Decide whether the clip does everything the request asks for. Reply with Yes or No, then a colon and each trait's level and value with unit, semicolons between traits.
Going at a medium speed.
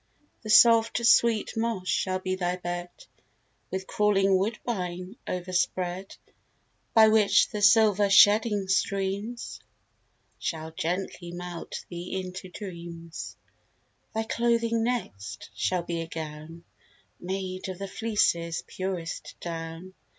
No: slow, 115 wpm